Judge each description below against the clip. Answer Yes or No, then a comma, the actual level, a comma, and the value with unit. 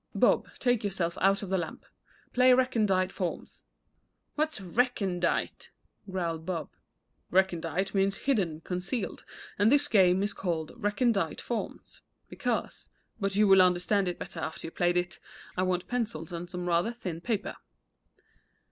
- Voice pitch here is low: No, high, 190 Hz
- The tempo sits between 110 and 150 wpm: Yes, average, 145 wpm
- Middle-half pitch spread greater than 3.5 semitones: No, average, 3.2 semitones